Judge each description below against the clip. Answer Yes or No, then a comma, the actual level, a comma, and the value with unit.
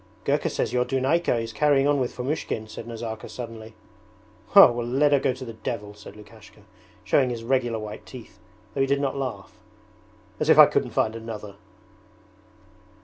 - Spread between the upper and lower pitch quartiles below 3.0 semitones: No, average, 3.3 semitones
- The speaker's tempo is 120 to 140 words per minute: No, average, 170 wpm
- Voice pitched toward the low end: Yes, low, 120 Hz